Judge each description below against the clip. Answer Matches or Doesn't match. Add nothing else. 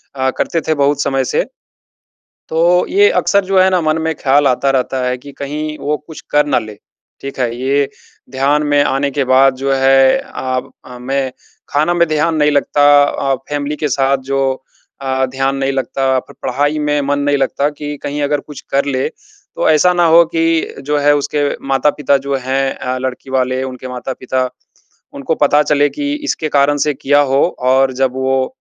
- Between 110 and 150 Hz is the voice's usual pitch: Matches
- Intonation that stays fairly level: Matches